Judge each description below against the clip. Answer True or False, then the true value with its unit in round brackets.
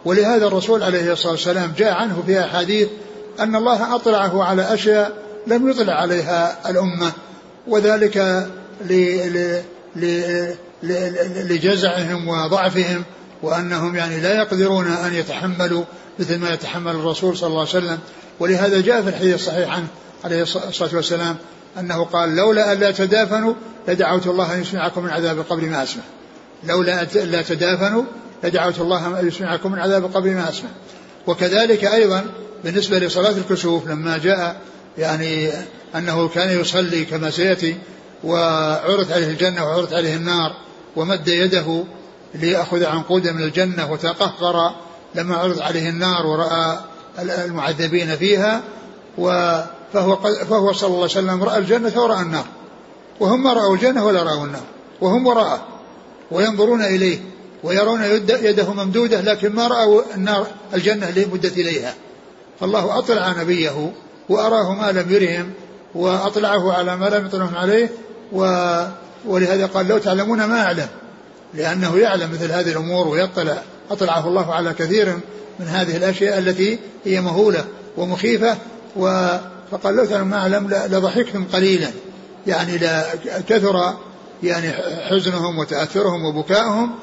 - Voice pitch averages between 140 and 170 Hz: False (185 Hz)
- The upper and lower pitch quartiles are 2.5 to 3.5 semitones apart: True (2.9 semitones)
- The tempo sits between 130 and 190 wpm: True (135 wpm)